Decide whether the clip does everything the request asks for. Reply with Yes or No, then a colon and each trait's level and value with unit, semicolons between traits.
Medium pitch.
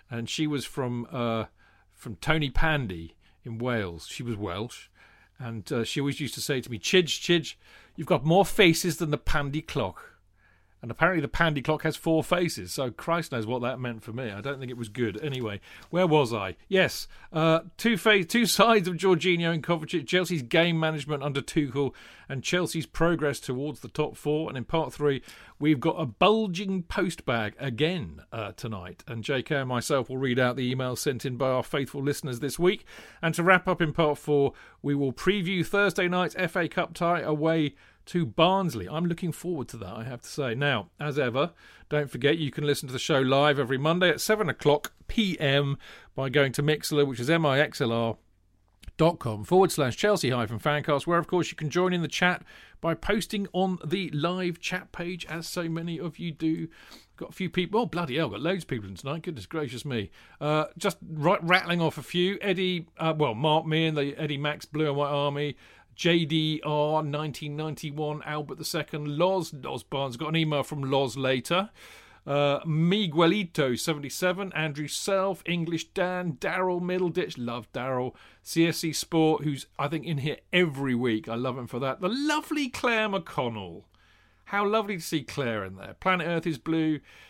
Yes: medium, 155 Hz